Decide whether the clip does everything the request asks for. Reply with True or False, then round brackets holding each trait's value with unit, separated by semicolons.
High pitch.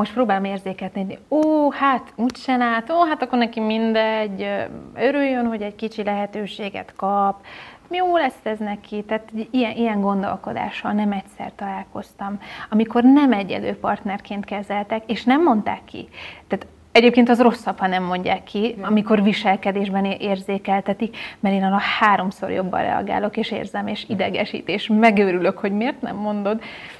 True (210 Hz)